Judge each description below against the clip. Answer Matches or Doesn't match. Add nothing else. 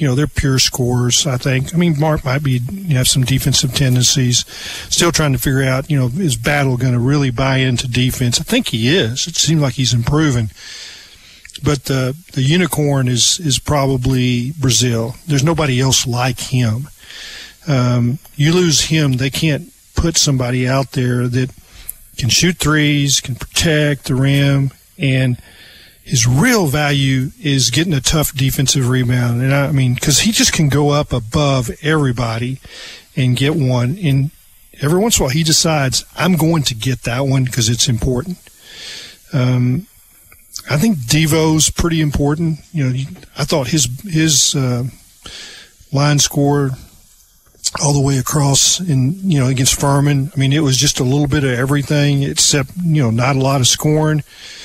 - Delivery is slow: Doesn't match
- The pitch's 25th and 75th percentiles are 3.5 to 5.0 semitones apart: Doesn't match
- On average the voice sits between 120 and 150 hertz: Matches